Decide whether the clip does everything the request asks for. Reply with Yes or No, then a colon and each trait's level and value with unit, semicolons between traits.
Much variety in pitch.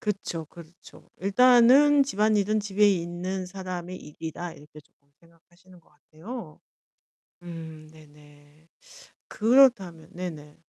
No: average, 4.7 semitones